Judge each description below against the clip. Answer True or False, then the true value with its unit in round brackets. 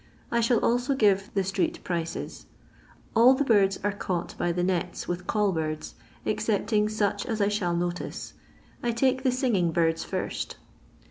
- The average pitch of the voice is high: True (205 Hz)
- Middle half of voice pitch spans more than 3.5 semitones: True (4.9 semitones)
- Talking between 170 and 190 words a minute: False (160 wpm)